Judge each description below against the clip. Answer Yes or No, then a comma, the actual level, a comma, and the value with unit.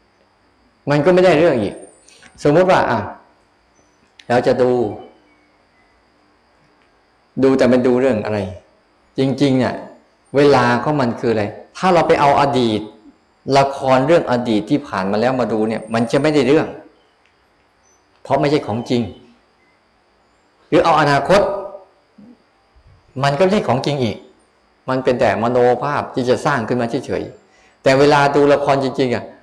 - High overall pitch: No, low, 130 Hz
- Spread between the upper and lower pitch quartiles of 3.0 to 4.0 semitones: Yes, average, 3.5 semitones